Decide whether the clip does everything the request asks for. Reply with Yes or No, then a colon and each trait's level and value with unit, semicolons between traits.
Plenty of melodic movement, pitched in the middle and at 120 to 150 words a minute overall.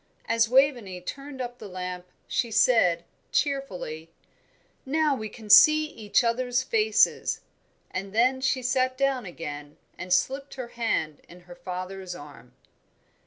No: wide, 6.2 semitones; high, 225 Hz; slow, 135 wpm